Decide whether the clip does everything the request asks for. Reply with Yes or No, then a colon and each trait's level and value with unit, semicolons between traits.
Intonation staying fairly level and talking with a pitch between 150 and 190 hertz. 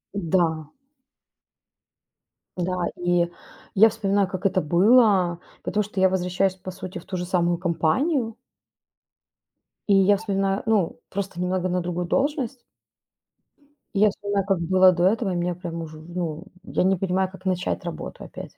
Yes: narrow, 2.2 semitones; medium, 185 Hz